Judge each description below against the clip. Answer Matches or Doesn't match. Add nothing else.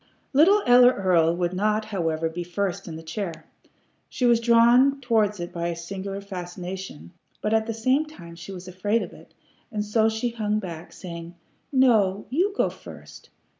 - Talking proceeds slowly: Doesn't match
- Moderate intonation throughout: Matches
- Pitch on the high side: Matches